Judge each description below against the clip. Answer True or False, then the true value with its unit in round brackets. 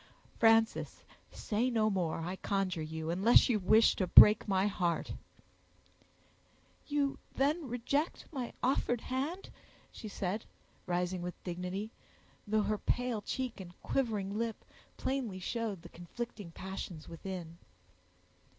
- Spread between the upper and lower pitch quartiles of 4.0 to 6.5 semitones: True (4.9 semitones)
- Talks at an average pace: False (125 wpm)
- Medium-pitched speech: False (210 Hz)